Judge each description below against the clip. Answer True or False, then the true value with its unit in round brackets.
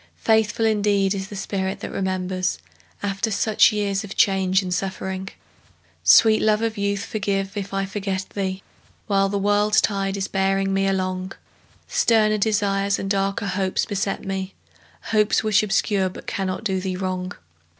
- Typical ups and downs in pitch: False (1.4 semitones)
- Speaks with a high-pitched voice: True (195 Hz)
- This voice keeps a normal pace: True (155 wpm)